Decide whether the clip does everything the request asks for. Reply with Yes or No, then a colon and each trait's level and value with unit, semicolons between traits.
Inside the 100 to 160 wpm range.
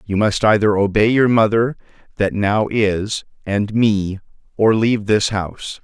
Yes: average, 155 wpm